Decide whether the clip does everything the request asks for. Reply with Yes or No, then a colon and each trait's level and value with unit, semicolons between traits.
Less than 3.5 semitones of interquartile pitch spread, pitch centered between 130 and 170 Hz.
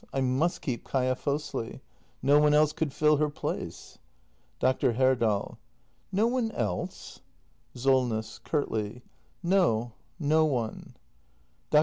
No: average, 4.0 semitones; low, 135 Hz